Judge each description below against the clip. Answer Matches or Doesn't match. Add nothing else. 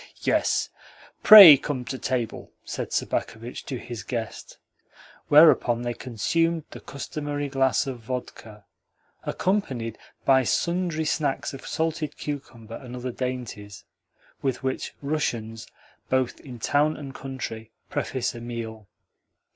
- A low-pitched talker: Matches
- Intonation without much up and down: Doesn't match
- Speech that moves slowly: Matches